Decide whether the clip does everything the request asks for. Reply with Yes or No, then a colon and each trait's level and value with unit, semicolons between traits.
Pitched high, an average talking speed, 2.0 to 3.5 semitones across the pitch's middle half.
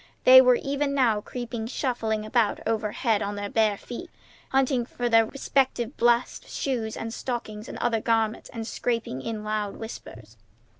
Yes: high, 230 Hz; average, 155 wpm; narrow, 2.5 semitones